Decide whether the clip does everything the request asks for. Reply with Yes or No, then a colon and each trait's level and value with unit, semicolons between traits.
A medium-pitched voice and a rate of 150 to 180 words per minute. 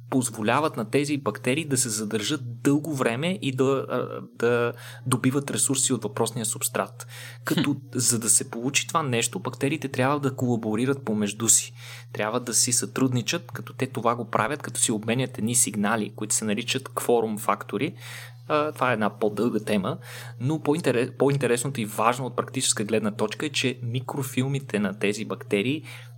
No: low, 120 Hz; average, 160 wpm